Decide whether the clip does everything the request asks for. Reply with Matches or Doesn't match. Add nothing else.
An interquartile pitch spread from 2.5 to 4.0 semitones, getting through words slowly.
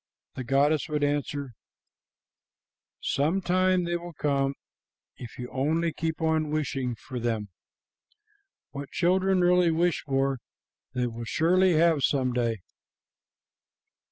Doesn't match